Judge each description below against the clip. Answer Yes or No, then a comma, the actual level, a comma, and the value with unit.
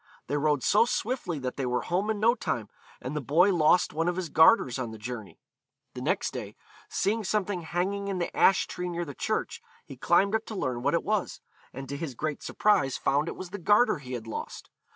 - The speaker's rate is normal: No, fast, 225 wpm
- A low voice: No, medium, 170 Hz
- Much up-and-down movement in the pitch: Yes, wide, 6.8 semitones